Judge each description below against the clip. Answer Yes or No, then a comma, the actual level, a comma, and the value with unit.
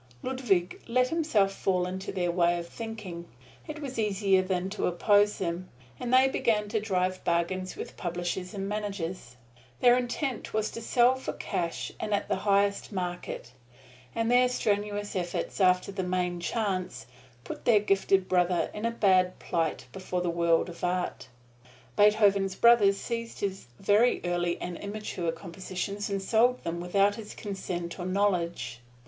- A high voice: Yes, high, 195 Hz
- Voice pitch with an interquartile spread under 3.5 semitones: Yes, average, 3.1 semitones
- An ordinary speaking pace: Yes, average, 155 wpm